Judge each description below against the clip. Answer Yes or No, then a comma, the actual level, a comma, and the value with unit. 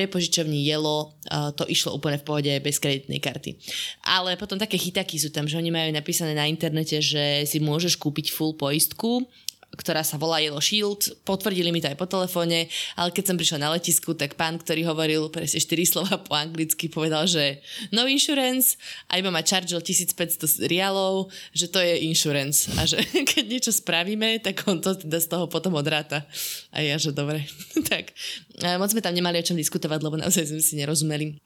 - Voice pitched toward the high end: No, medium, 165 Hz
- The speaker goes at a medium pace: No, fast, 185 wpm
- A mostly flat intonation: No, average, 3.2 semitones